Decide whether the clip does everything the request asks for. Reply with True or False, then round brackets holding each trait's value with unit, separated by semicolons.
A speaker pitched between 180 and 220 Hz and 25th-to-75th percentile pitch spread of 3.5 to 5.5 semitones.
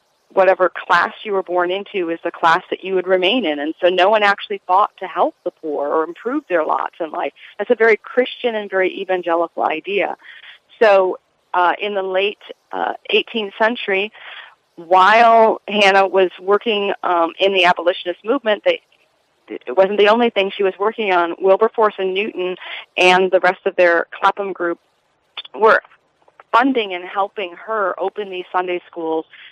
False (190 Hz; 2.8 semitones)